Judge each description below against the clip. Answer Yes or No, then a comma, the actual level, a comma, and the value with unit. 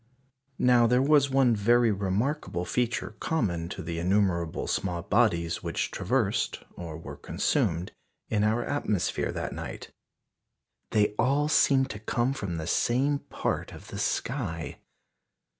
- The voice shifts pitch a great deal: Yes, wide, 6.5 semitones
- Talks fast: No, slow, 135 wpm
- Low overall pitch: Yes, low, 110 Hz